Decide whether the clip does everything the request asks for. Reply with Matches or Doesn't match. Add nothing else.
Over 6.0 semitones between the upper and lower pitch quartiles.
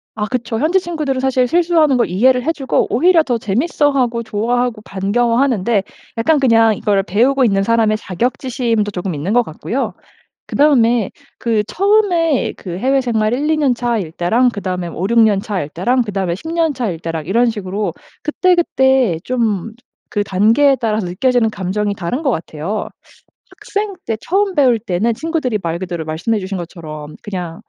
Doesn't match